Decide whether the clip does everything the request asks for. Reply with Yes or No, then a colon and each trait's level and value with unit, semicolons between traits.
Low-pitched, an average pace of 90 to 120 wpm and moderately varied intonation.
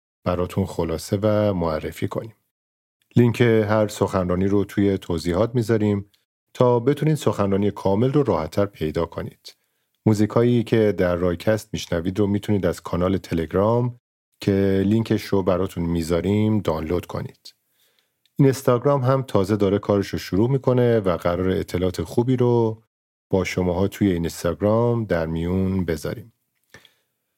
No: low, 100 Hz; average, 130 wpm; average, 4.1 semitones